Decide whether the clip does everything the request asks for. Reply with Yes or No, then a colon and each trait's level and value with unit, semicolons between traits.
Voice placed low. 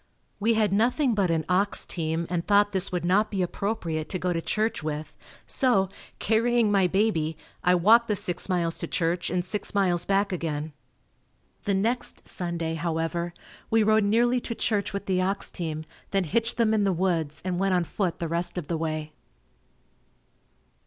No: medium, 185 Hz